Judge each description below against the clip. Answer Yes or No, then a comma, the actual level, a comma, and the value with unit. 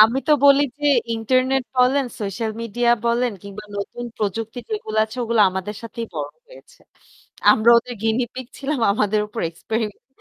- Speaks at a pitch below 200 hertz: No, high, 230 Hz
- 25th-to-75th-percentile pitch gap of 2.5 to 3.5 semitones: Yes, average, 2.9 semitones